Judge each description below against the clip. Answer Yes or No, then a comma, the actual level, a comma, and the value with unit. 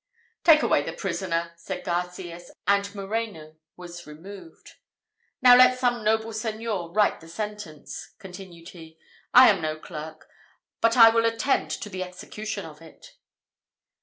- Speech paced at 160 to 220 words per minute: No, average, 140 wpm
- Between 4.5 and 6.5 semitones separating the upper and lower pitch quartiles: Yes, average, 4.8 semitones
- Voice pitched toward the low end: No, high, 195 Hz